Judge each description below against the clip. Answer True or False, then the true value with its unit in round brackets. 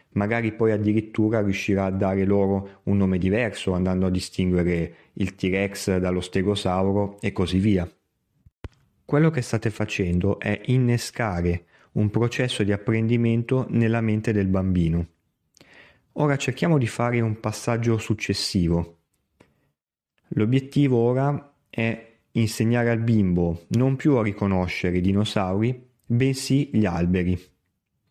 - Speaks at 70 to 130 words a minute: True (120 wpm)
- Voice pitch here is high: False (105 Hz)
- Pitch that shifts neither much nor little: True (3.9 semitones)